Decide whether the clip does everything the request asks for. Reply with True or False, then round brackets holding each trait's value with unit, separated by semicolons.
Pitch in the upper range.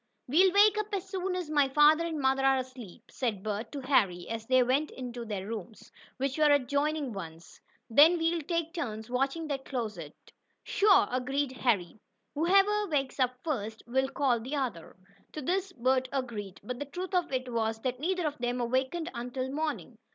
True (265 Hz)